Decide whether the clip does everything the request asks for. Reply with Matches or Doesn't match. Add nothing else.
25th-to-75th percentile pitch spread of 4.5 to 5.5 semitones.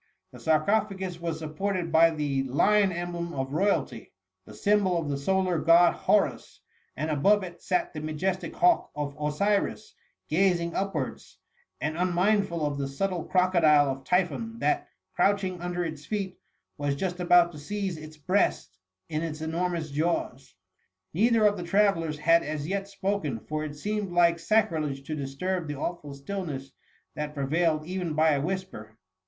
Doesn't match